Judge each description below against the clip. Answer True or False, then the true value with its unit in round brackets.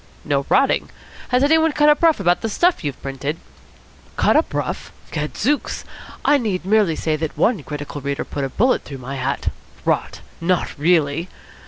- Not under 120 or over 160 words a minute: False (175 wpm)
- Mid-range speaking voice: True (170 Hz)